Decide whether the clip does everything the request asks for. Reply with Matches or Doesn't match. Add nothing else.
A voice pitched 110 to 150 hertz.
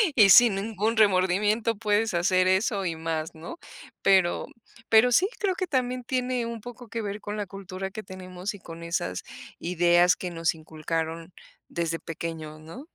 Doesn't match